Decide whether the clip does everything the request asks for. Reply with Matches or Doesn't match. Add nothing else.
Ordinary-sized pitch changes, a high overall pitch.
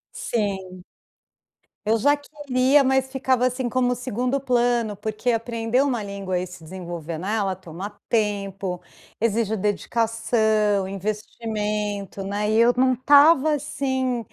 Matches